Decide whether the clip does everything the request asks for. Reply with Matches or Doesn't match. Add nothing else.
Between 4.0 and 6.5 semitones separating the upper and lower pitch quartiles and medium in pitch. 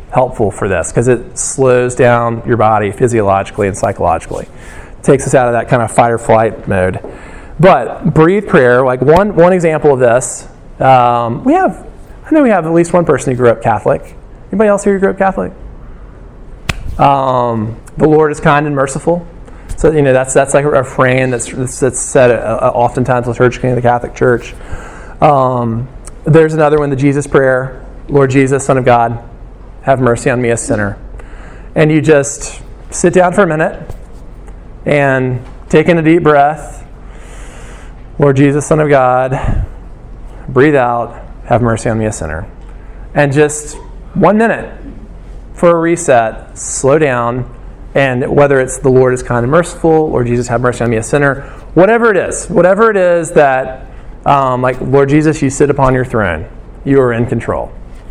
Doesn't match